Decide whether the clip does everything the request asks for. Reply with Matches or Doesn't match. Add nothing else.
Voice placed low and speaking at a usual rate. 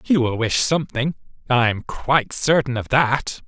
Matches